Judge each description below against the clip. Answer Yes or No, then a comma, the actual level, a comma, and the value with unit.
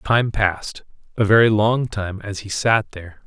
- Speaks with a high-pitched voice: No, low, 105 Hz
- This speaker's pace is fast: No, average, 185 wpm